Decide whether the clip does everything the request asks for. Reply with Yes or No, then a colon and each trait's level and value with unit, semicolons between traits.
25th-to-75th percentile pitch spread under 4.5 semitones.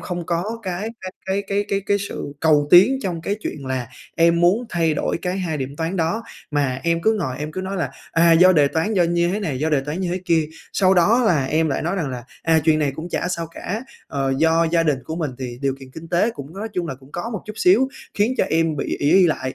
Yes: average, 4.0 semitones